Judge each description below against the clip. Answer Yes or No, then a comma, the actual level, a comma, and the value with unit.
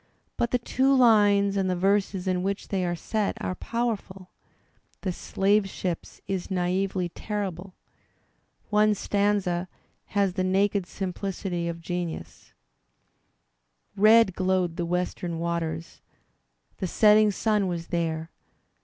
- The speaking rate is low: Yes, slow, 125 wpm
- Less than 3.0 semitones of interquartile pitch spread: Yes, narrow, 2.5 semitones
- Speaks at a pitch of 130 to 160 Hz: No, high, 190 Hz